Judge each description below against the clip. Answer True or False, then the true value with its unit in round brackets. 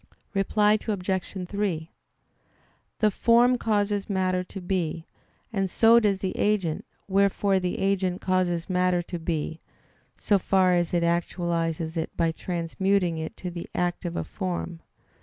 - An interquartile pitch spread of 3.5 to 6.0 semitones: False (2.5 semitones)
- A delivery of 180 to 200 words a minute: False (140 wpm)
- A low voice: False (185 Hz)